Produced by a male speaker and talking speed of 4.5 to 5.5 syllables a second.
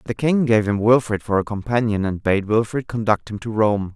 Yes: male; 5.3 syllables/s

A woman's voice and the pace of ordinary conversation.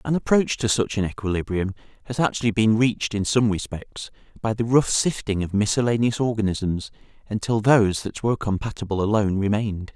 No: male; average, 165 wpm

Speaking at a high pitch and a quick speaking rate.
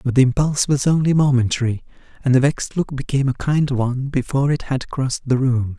No: low, 135 Hz; fast, 210 wpm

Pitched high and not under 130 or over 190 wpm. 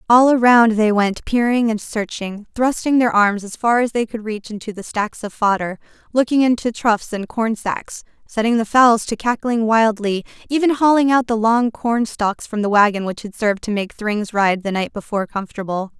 No: high, 220 Hz; fast, 205 wpm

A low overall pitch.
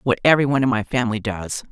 Yes: low, 120 Hz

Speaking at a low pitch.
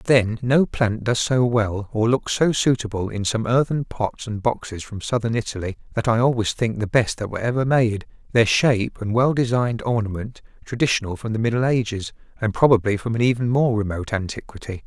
Yes: low, 115 Hz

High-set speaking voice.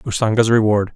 No: low, 110 Hz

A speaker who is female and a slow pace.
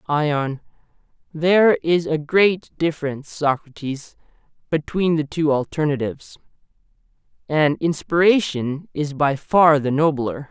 No: male; slow, 105 wpm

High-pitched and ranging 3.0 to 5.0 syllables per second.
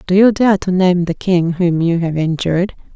No: medium, 180 Hz; 4.9 syllables/s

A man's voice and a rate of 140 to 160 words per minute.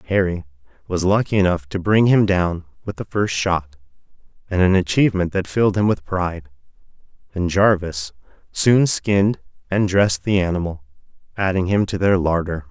Yes: male; average, 150 wpm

